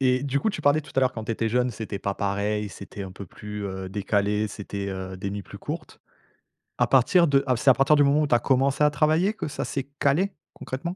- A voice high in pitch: No, low, 125 Hz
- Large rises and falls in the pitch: Yes, wide, 5.8 semitones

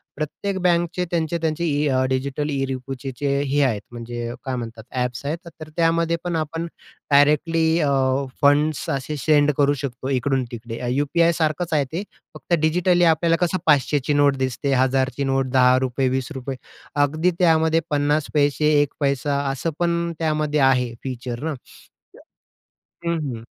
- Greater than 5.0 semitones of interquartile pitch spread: No, average, 3.5 semitones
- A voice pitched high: No, medium, 145 Hz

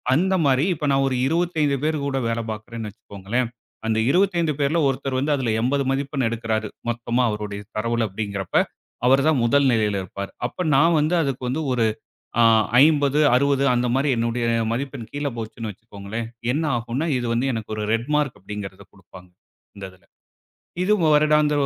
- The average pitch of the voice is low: Yes, low, 125 Hz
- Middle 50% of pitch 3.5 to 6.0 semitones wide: Yes, average, 4.5 semitones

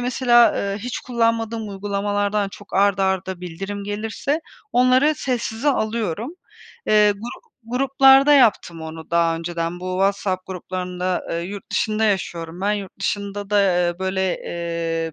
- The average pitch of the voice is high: Yes, high, 200 Hz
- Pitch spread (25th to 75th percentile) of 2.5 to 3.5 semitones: No, average, 3.9 semitones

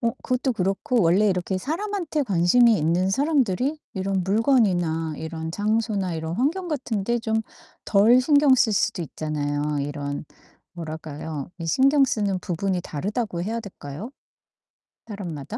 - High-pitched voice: Yes, high, 195 Hz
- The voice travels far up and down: Yes, wide, 6.6 semitones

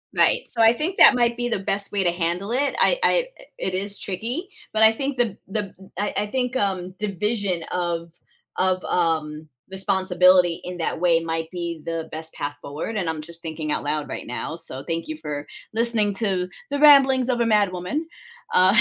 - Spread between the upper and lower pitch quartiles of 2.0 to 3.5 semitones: No, average, 5.2 semitones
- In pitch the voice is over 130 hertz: Yes, medium, 185 Hz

